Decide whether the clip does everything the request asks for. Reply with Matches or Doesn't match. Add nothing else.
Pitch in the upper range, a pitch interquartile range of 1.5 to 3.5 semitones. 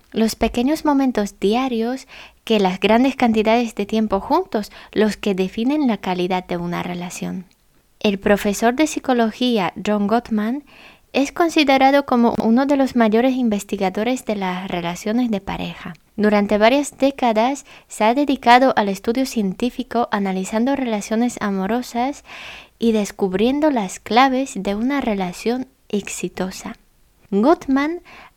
Doesn't match